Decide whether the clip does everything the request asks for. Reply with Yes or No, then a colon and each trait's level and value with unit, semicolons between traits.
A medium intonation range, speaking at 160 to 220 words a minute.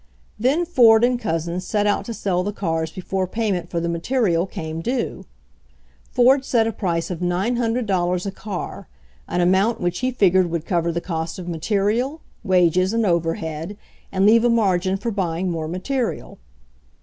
Yes: average, 4.8 semitones; average, 165 wpm